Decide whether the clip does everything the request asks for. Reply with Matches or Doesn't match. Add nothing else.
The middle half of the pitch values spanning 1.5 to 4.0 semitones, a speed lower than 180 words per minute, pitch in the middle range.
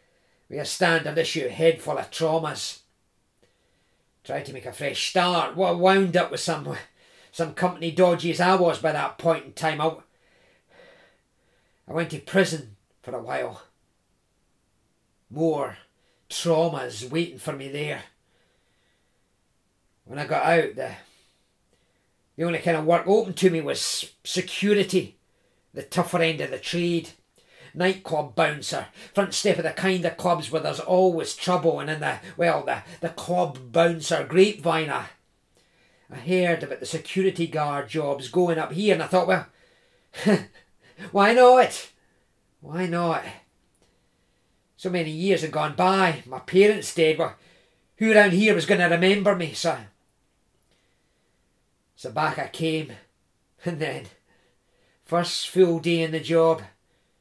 Matches